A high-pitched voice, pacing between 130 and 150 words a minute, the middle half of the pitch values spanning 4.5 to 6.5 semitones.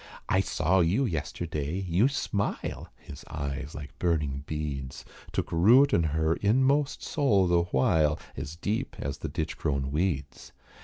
No: very low, 80 Hz; average, 145 wpm; average, 5.0 semitones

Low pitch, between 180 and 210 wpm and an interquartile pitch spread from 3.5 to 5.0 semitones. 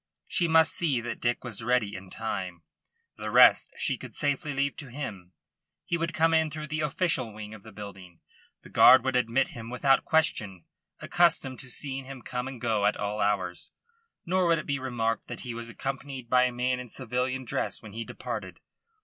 Yes: low, 125 Hz; average, 200 wpm; average, 4.2 semitones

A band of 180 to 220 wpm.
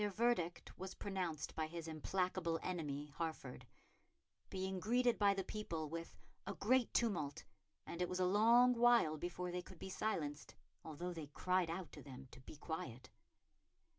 No: average, 165 wpm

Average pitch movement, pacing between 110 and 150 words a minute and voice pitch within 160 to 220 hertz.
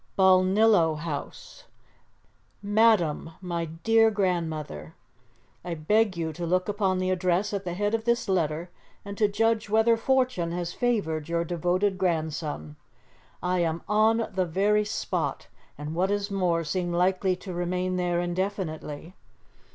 Yes: average, 3.4 semitones; average, 140 wpm; medium, 185 Hz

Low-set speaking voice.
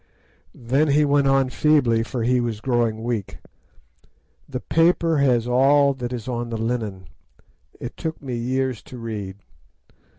Yes: low, 125 Hz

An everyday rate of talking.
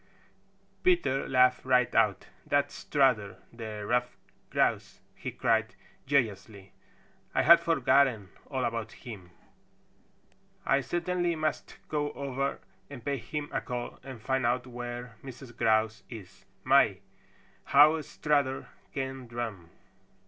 No: slow, 120 wpm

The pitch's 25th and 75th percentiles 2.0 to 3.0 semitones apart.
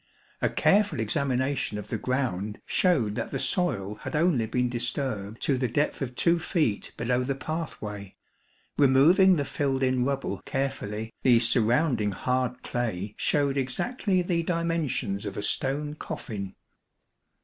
No: average, 5.3 semitones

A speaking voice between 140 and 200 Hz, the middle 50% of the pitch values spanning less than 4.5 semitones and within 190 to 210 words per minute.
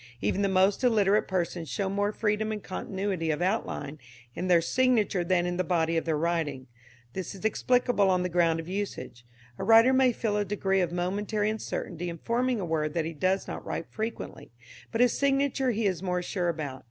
Yes: high, 190 Hz; average, 4.1 semitones; average, 200 wpm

